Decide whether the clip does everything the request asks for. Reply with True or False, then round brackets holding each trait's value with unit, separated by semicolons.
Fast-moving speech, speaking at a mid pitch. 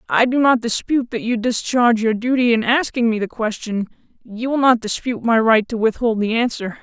False (210 wpm; 230 Hz)